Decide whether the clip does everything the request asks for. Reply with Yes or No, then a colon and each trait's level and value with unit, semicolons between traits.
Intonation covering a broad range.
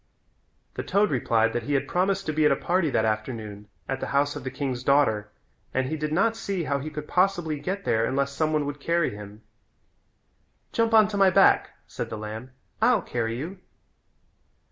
Yes: wide, 7.0 semitones